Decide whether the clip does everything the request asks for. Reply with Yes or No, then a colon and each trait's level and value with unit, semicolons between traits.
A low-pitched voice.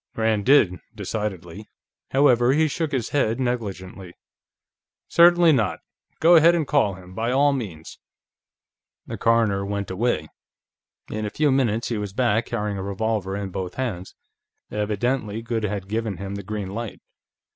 Yes: low, 110 Hz